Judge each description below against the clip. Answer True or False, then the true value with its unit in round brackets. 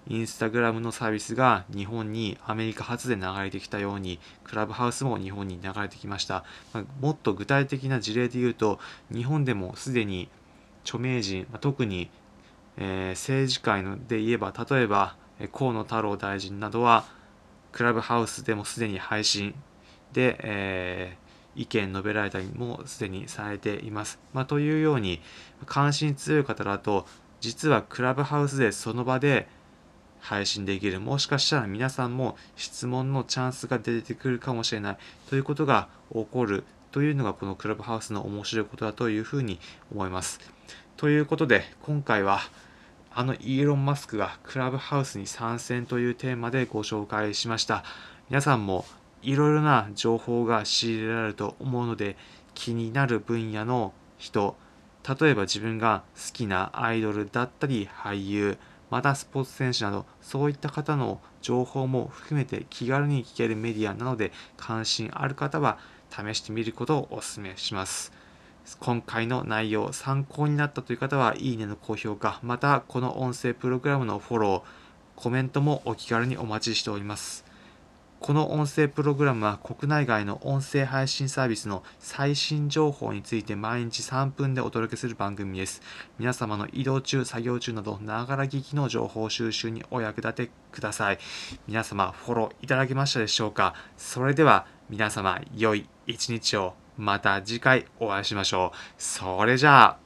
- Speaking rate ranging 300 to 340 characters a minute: True (335 characters per minute)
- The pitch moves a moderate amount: True (4.2 semitones)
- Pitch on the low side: True (115 Hz)